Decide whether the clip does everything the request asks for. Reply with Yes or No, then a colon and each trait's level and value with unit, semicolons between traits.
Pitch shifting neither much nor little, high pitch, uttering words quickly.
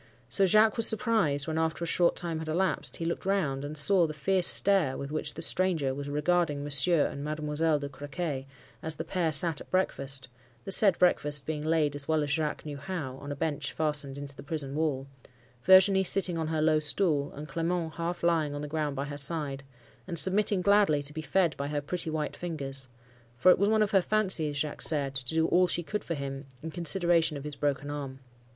No: average, 3.4 semitones; medium, 155 Hz; fast, 215 wpm